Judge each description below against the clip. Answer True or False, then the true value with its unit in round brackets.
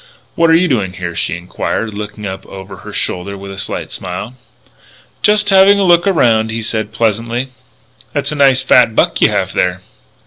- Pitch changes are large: True (6.6 semitones)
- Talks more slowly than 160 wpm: False (185 wpm)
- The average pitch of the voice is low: True (110 Hz)